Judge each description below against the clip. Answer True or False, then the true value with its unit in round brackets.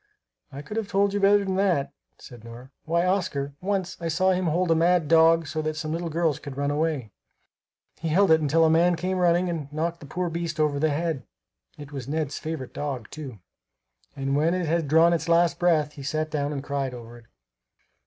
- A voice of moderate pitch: True (160 Hz)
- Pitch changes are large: False (3.3 semitones)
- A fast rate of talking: True (220 wpm)